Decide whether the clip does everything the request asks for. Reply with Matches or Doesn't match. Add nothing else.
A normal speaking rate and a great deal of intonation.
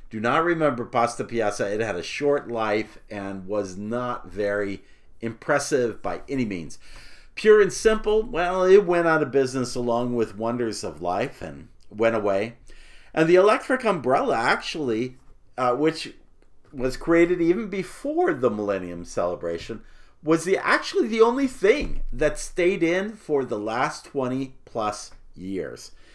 Matches